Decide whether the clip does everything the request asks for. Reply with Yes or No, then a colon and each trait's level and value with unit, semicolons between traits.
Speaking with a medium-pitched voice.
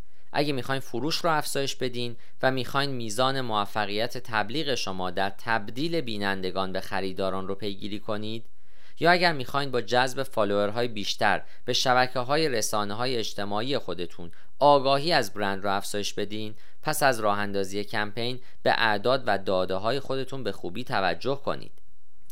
No: low, 115 Hz